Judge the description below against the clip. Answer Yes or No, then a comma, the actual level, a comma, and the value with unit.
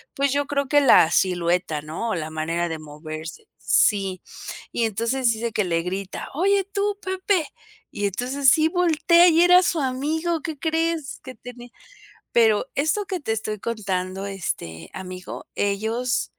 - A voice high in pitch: Yes, high, 235 Hz